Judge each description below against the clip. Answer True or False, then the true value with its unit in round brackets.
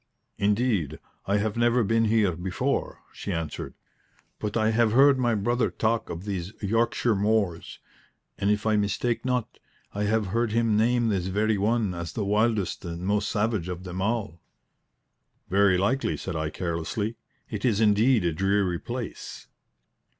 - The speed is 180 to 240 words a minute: False (160 wpm)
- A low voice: True (105 Hz)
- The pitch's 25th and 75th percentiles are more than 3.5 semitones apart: False (3.2 semitones)